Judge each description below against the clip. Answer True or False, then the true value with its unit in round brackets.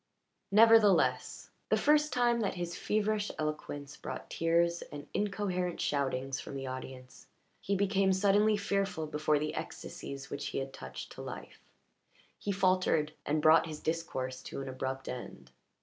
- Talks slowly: False (150 wpm)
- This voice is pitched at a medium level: True (165 Hz)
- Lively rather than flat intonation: True (6.4 semitones)